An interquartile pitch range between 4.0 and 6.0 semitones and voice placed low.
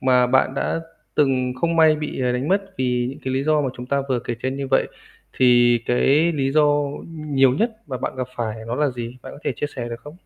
No: average, 3.1 semitones; low, 130 Hz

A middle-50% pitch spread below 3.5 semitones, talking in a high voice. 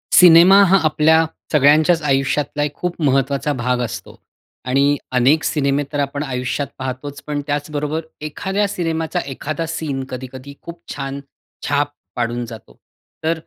No: average, 3.0 semitones; medium, 145 Hz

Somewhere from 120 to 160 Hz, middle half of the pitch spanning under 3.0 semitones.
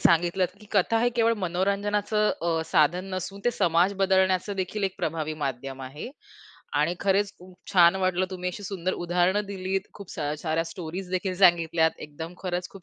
No: medium, 185 Hz; narrow, 2.6 semitones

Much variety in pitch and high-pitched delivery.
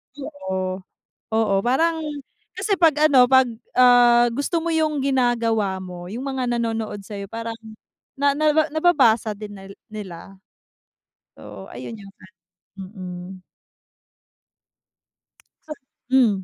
Yes: wide, 5.7 semitones; high, 230 Hz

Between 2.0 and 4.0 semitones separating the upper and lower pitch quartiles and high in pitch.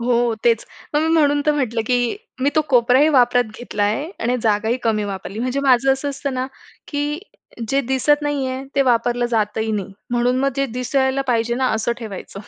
Yes: average, 3.1 semitones; very high, 250 Hz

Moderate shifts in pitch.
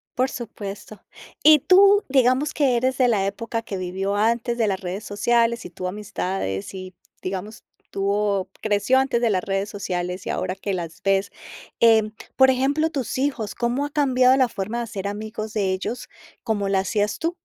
Yes: average, 4.4 semitones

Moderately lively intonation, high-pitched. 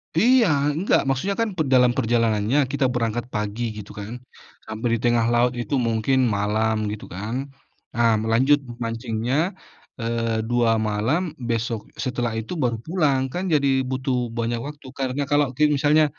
No: average, 3.5 semitones; low, 120 Hz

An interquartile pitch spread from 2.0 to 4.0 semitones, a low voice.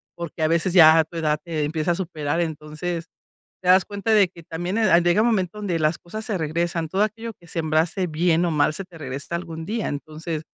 No: average, 2.8 semitones; medium, 170 Hz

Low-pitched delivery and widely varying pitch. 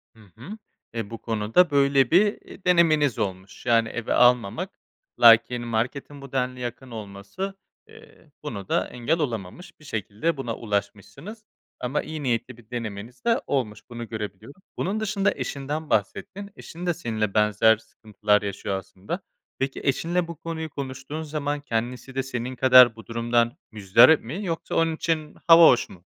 Yes: low, 125 Hz; wide, 5.9 semitones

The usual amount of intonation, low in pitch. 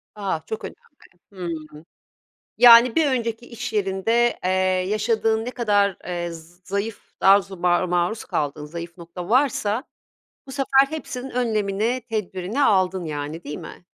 No: average, 5.0 semitones; high, 205 Hz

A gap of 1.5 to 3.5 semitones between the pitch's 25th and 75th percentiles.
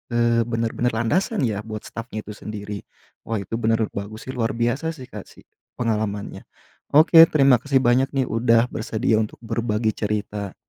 Yes: narrow, 2.4 semitones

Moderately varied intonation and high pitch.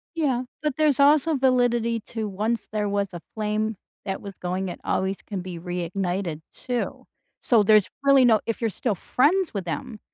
Yes: average, 4.7 semitones; high, 215 Hz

